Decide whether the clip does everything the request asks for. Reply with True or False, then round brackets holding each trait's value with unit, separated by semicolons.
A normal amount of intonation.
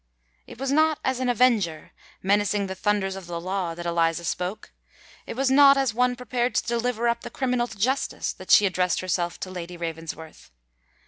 False (5.9 semitones)